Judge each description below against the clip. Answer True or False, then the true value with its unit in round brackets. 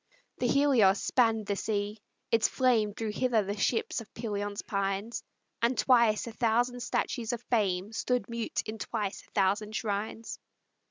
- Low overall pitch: False (220 Hz)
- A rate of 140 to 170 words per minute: True (155 wpm)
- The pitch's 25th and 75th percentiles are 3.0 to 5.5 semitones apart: False (2.6 semitones)